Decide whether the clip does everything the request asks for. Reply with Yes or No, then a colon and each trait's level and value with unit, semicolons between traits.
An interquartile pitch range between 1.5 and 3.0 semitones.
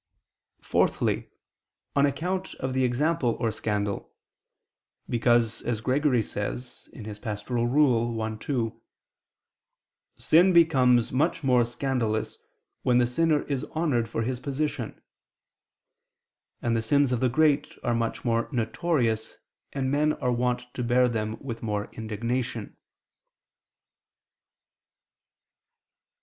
No: average, 3.4 semitones